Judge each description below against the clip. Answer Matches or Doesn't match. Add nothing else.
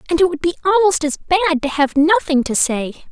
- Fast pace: Matches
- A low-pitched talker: Doesn't match